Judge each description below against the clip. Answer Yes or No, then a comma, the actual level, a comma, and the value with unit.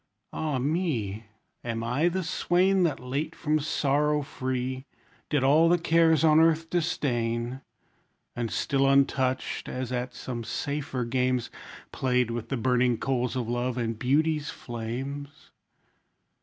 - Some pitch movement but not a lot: Yes, average, 3.8 semitones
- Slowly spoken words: Yes, slow, 130 wpm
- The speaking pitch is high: No, low, 130 Hz